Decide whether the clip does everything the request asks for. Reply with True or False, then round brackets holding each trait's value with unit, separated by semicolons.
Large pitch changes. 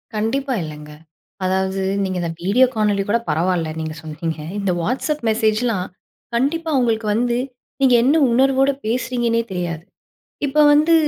True (5.9 semitones)